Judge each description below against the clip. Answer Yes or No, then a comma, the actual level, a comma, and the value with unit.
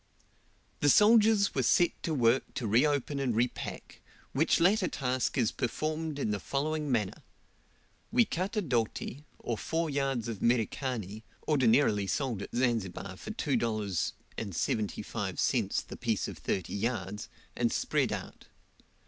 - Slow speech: Yes, slow, 130 wpm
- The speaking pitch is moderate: No, low, 125 Hz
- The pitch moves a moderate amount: No, wide, 5.8 semitones